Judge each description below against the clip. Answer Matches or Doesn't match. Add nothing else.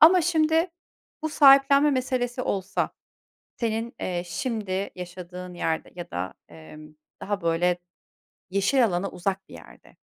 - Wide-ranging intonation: Matches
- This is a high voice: Matches